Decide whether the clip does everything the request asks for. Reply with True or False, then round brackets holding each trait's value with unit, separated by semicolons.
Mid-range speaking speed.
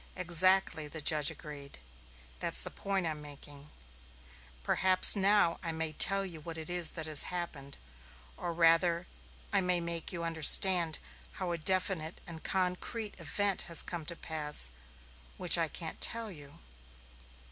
True (145 wpm)